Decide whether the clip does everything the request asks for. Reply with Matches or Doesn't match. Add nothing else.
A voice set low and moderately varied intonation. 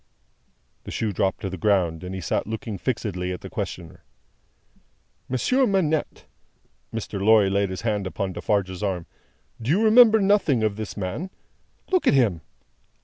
Doesn't match